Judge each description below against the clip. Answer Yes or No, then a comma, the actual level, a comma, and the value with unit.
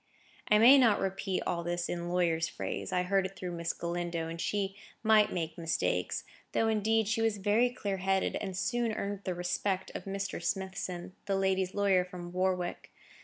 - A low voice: No, high, 190 Hz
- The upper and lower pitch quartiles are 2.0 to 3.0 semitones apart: Yes, narrow, 2.6 semitones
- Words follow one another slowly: No, average, 180 wpm